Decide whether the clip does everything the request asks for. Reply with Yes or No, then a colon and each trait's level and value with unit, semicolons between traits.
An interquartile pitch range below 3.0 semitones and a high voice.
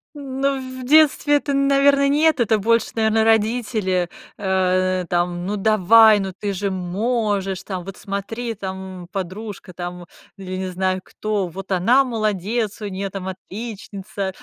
No: average, 3.5 semitones; high, 200 Hz